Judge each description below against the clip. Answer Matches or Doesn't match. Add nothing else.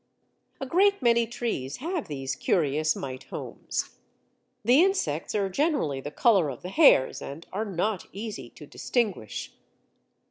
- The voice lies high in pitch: Matches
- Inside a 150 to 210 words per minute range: Doesn't match